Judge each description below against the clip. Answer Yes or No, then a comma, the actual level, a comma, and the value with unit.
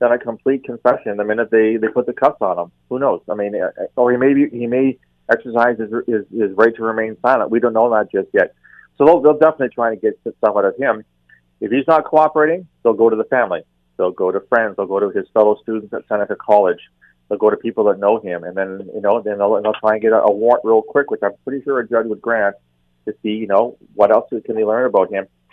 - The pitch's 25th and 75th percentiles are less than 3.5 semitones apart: Yes, narrow, 2.6 semitones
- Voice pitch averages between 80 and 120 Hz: Yes, low, 115 Hz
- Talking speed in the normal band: No, fast, 265 wpm